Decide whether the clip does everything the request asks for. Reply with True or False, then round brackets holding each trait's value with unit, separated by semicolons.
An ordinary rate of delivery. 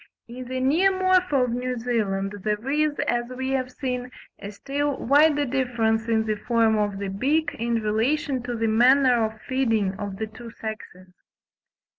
True (165 wpm)